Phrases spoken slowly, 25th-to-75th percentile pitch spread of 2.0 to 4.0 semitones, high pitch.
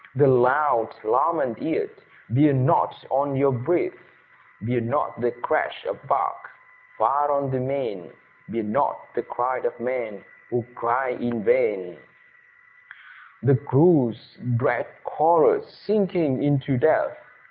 No: slow, 125 wpm; average, 3.5 semitones; low, 135 Hz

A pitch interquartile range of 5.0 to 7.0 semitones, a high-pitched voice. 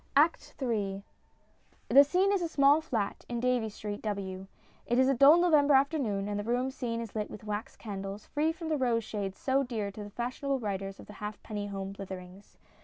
Yes: average, 5.3 semitones; high, 230 Hz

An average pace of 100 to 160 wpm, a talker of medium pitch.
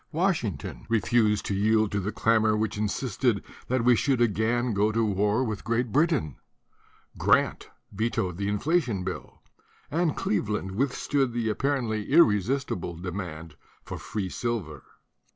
No: average, 140 wpm; low, 110 Hz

